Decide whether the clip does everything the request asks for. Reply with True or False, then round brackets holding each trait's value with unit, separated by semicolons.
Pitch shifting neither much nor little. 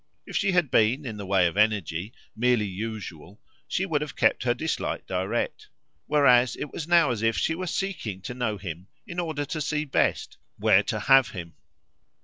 False (6.7 semitones)